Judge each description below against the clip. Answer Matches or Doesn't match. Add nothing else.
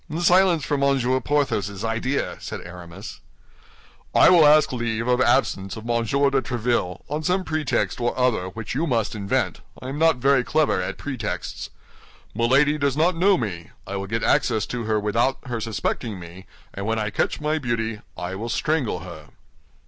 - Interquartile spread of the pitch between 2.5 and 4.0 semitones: Doesn't match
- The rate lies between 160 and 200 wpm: Matches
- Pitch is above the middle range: Doesn't match